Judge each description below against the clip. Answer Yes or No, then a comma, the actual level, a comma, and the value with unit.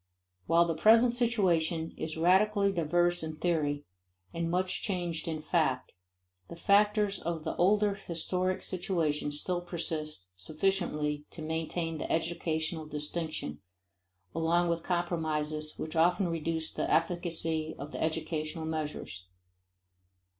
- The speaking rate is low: Yes, slow, 120 wpm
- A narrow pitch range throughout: Yes, narrow, 2.2 semitones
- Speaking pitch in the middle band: Yes, medium, 165 Hz